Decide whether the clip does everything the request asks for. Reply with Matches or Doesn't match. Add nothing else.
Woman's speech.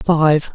Matches